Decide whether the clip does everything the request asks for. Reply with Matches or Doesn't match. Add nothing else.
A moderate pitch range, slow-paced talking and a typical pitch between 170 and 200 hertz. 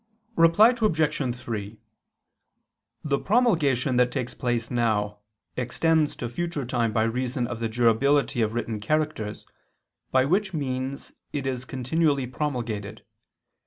Doesn't match